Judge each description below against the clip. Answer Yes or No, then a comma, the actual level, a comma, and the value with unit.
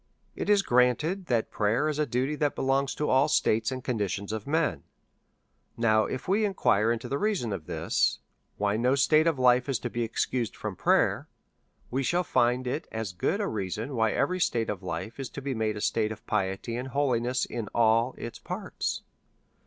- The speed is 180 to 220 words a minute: Yes, average, 190 wpm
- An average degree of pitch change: Yes, average, 4.1 semitones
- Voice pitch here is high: No, low, 125 Hz